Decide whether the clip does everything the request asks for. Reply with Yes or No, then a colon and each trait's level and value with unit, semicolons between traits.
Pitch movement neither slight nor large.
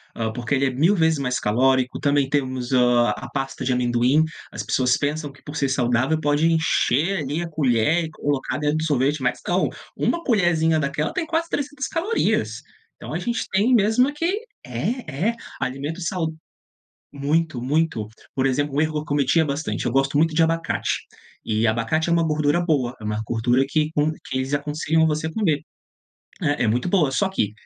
Yes: average, 4.0 semitones